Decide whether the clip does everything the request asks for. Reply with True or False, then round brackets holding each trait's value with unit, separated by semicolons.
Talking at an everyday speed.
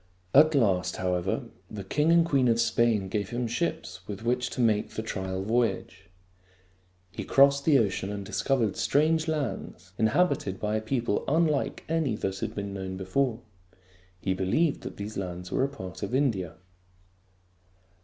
True (160 wpm)